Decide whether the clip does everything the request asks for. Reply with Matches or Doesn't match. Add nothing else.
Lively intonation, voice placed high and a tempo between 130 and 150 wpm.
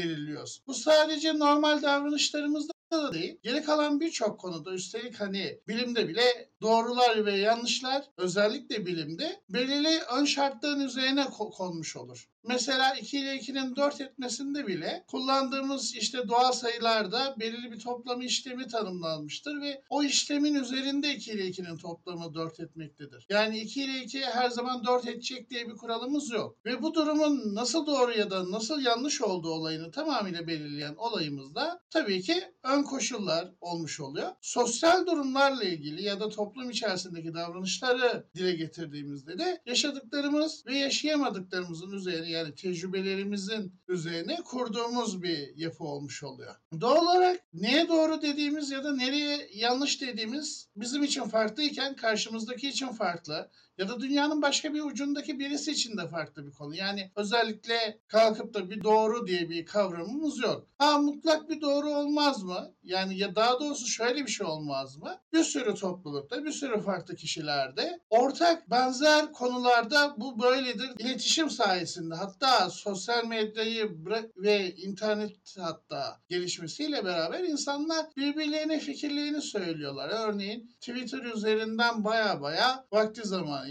Matches